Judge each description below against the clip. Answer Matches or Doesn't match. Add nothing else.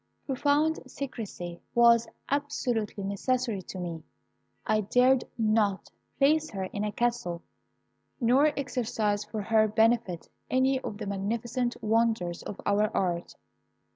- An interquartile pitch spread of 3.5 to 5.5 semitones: Matches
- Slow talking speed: Matches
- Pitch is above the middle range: Matches